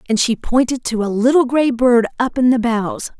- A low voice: No, high, 240 Hz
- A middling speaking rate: No, fast, 225 wpm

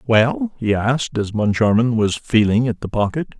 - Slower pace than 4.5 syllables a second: No, 4.9 syllables/s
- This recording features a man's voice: Yes, male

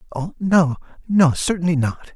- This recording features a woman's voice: No, male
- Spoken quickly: No, average, 140 wpm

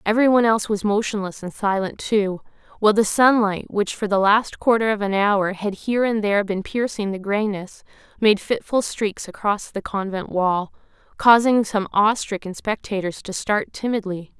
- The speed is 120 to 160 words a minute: No, average, 175 wpm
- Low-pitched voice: No, high, 205 Hz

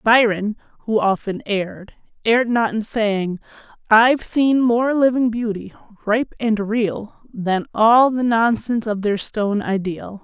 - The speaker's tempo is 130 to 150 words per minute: Yes, average, 140 wpm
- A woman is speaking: Yes, female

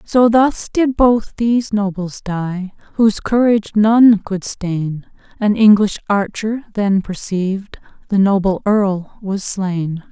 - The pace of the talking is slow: Yes, slow, 130 wpm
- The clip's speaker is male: No, female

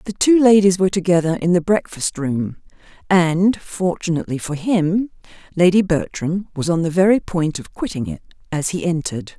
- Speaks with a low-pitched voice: No, medium, 175 Hz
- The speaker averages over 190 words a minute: No, average, 165 wpm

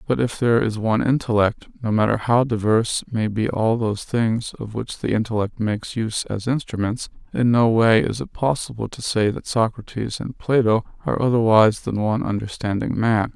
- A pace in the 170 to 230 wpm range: Yes, average, 185 wpm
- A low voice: Yes, low, 115 Hz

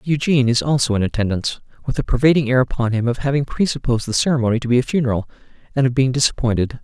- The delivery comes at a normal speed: No, fast, 210 wpm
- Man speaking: Yes, male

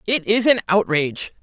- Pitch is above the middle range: Yes, high, 195 Hz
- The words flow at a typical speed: Yes, average, 170 wpm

